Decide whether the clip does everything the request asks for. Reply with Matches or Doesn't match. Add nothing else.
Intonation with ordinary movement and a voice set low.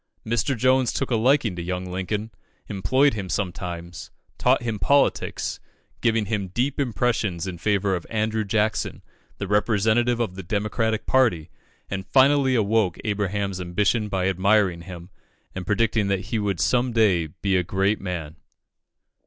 Matches